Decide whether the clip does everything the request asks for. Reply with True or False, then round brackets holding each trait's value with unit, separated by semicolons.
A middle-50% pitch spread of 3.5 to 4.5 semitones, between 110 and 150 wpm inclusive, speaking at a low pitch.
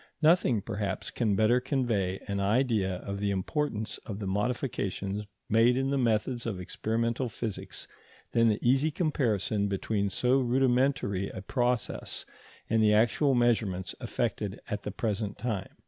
True (3.8 semitones; 145 wpm; 110 Hz)